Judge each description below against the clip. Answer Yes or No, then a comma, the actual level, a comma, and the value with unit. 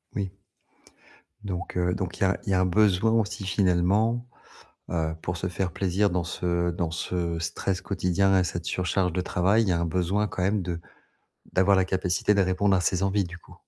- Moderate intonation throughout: No, narrow, 2.1 semitones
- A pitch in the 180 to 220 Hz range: No, very low, 95 Hz